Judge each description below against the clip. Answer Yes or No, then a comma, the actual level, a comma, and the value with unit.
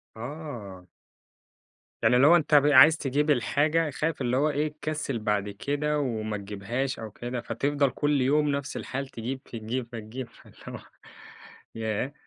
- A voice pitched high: No, low, 130 Hz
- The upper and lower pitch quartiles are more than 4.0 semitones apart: Yes, average, 4.4 semitones